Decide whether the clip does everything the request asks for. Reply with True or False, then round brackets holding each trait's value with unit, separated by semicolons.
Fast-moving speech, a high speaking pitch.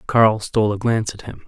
False (245 wpm; 110 Hz)